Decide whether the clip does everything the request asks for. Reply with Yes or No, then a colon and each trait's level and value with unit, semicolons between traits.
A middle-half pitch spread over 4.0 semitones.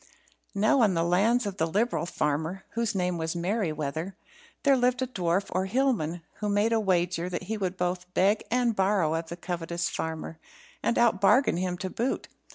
Yes: average, 4.4 semitones